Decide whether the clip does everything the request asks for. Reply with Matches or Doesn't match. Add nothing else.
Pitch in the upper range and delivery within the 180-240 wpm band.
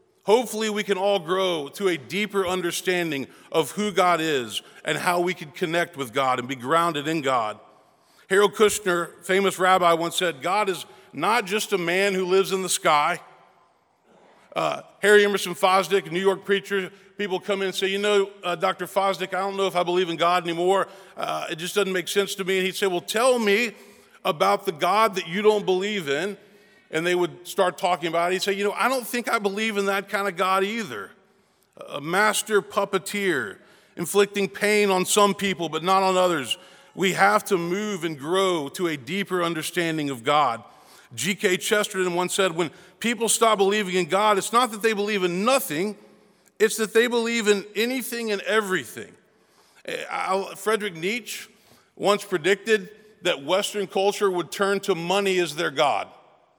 Matches